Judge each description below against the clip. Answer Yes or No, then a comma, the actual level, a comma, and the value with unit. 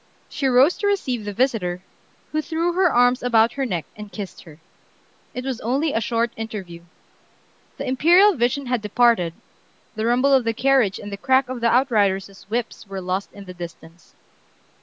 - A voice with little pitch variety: No, average, 4.8 semitones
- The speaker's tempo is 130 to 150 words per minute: No, average, 180 wpm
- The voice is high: Yes, high, 235 Hz